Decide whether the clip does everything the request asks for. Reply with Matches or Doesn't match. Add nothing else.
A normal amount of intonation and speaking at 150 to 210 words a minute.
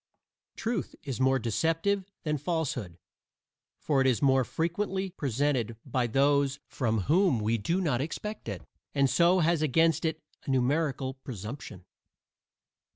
Doesn't match